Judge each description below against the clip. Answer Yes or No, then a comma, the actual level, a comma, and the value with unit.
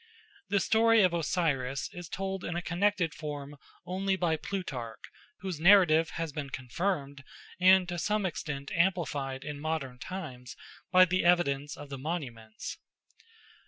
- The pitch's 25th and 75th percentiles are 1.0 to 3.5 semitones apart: No, average, 4.7 semitones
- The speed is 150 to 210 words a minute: No, average, 140 wpm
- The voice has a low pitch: No, medium, 165 Hz